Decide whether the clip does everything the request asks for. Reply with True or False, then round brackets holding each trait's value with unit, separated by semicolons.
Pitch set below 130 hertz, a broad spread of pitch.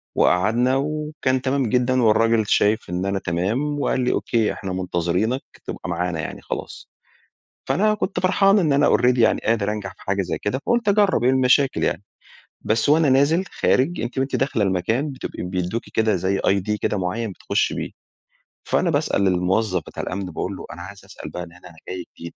True (110 Hz; 6.1 semitones)